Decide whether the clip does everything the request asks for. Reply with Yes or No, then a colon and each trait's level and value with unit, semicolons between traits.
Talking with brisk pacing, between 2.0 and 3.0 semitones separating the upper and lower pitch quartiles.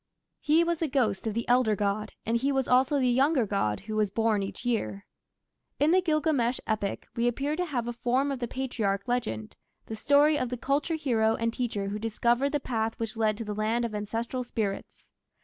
No: fast, 210 wpm; average, 4.0 semitones